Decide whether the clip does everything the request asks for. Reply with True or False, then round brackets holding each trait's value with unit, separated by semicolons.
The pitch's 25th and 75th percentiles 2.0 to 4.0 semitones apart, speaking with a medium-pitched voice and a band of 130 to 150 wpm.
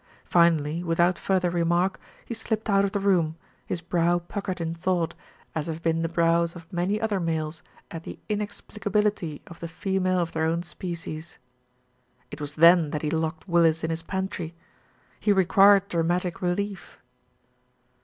False (2.6 semitones; 175 Hz; 160 wpm)